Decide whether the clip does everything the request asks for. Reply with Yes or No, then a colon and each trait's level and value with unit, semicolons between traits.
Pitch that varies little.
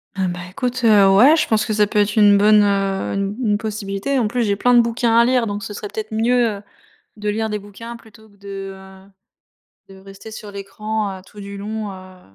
Yes: narrow, 2.0 semitones